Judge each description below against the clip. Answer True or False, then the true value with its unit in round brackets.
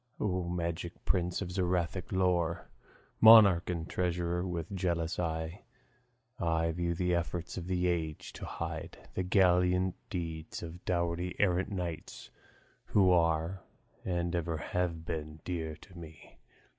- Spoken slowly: True (130 wpm)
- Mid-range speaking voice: False (85 Hz)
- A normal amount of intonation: False (1.6 semitones)